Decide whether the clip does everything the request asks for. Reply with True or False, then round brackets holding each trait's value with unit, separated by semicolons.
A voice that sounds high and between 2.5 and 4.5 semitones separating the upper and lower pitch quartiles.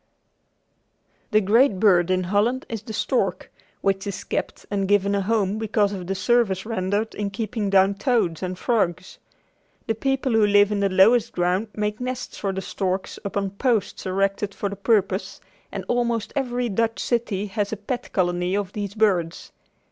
True (205 Hz; 2.8 semitones)